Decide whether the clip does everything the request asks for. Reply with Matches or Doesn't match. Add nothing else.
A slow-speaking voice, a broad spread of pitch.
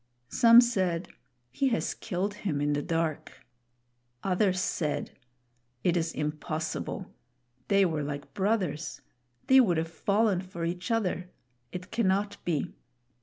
Doesn't match